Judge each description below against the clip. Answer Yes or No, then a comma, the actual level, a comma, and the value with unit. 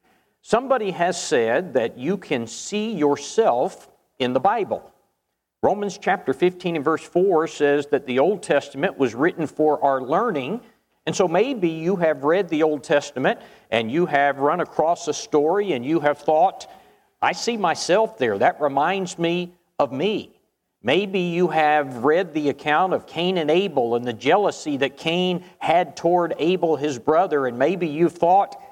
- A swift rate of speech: No, average, 165 wpm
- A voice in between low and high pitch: Yes, medium, 170 Hz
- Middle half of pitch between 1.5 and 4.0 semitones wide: No, average, 4.5 semitones